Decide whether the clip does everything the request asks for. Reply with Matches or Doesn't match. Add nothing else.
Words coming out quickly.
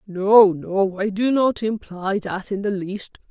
Doesn't match